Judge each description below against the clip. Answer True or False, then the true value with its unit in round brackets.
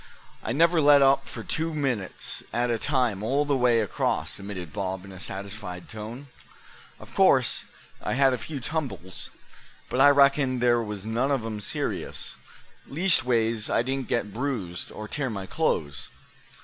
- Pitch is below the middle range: True (120 Hz)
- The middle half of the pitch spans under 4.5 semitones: False (5.1 semitones)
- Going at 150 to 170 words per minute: True (160 wpm)